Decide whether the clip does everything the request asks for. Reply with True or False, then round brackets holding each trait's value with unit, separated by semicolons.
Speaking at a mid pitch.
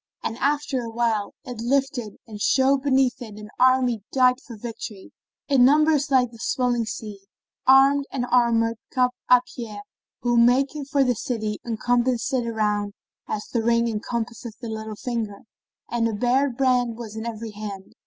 False (240 Hz)